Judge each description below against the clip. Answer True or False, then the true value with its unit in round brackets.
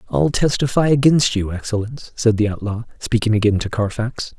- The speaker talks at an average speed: True (165 wpm)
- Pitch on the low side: True (115 Hz)